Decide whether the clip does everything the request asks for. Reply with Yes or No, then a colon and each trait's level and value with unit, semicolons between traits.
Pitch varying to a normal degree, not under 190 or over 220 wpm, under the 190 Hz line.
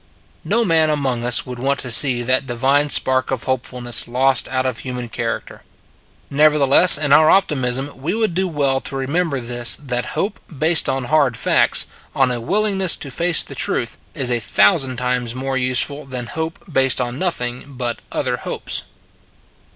No: average, 3.3 semitones; average, 175 wpm; low, 135 Hz